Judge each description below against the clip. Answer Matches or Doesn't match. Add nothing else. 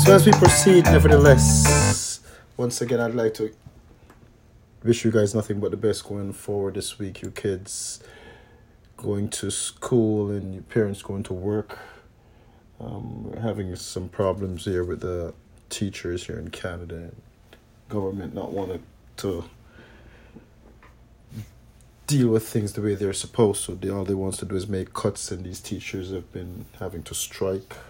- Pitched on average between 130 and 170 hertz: Doesn't match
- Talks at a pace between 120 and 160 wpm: Matches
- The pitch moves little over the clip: Doesn't match